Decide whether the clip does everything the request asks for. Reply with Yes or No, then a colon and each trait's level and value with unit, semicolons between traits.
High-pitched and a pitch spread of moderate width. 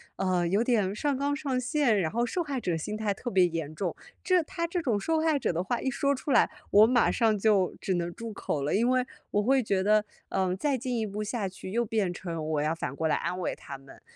No: high, 215 Hz; wide, 5.8 semitones